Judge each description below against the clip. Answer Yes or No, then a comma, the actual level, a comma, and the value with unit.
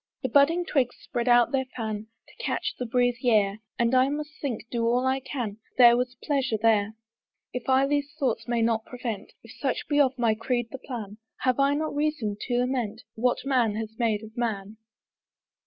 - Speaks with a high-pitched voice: Yes, high, 245 Hz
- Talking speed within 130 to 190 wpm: No, average, 200 wpm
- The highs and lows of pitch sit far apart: No, average, 3.0 semitones